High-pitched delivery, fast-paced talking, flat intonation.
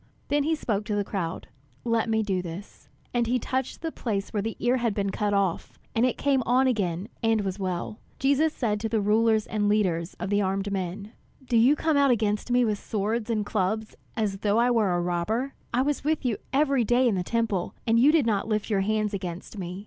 No: high, 215 Hz; fast, 225 wpm; average, 3.5 semitones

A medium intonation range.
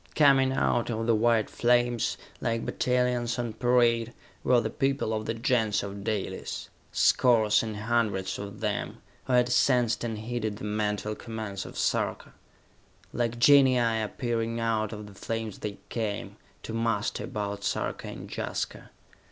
No: narrow, 2.2 semitones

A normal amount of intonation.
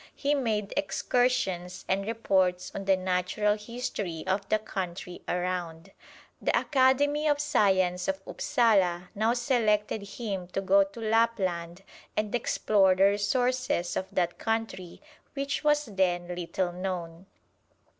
Yes: average, 4.1 semitones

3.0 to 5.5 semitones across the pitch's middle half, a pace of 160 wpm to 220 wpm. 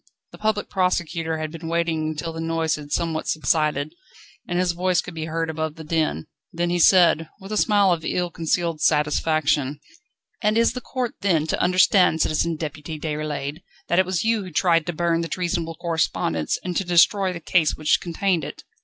No: narrow, 2.4 semitones; average, 190 wpm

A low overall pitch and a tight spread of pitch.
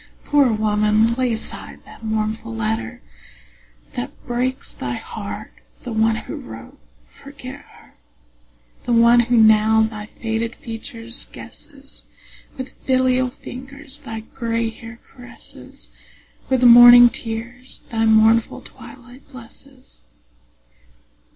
No: high, 230 Hz; narrow, 2.3 semitones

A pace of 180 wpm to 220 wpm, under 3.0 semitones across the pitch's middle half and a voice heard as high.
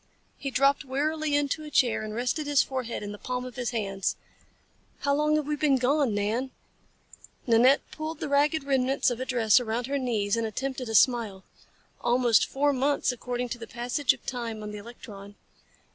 No: average, 190 wpm; average, 3.6 semitones; very high, 250 Hz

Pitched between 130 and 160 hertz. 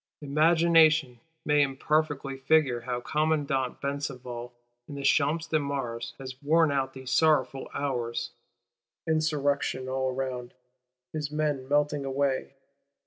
Yes: medium, 140 Hz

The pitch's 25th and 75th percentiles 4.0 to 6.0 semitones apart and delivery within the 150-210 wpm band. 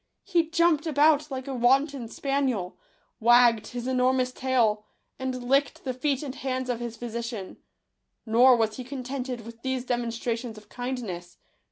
No: narrow, 2.4 semitones; average, 155 wpm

